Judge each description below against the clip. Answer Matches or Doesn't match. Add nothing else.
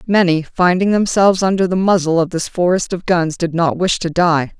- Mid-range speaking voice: Matches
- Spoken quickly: Matches